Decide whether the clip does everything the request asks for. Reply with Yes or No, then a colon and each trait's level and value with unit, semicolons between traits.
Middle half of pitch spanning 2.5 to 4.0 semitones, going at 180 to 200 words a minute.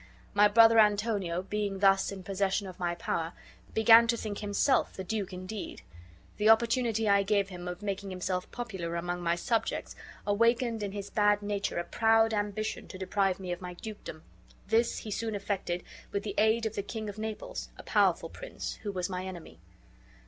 Yes: average, 2.9 semitones; average, 185 wpm